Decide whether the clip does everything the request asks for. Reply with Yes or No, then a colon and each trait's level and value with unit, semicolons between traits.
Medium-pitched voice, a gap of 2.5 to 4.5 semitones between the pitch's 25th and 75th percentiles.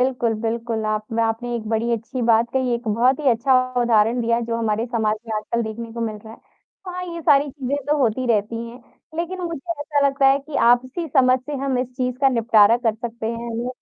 No: high, 235 Hz; average, 2.9 semitones